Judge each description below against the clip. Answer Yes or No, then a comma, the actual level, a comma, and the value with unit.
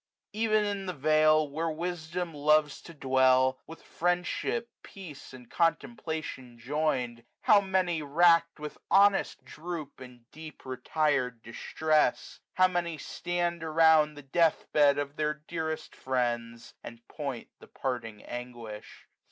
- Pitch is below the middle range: No, medium, 155 Hz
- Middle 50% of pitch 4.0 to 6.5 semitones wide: Yes, average, 4.6 semitones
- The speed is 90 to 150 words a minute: Yes, slow, 135 wpm